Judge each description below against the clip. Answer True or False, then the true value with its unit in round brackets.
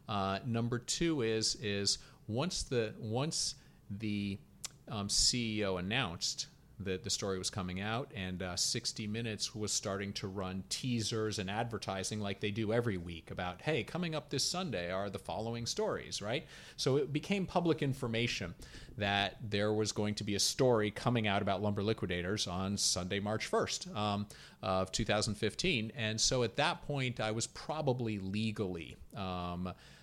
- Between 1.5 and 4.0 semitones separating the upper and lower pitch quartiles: True (3.5 semitones)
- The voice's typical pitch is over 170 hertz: False (110 Hz)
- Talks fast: False (160 wpm)